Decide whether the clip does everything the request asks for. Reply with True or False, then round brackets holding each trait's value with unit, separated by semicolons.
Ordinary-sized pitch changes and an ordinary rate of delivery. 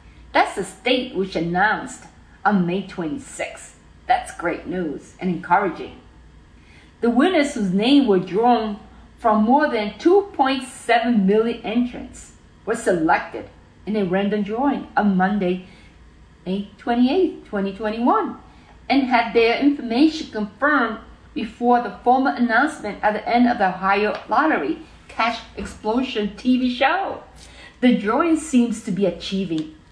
False (4.9 semitones; 125 wpm)